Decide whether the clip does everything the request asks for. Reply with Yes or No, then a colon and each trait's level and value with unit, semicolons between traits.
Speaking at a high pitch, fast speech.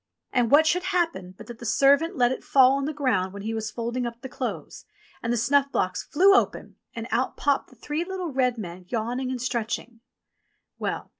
Yes: very high, 250 Hz; fast, 215 wpm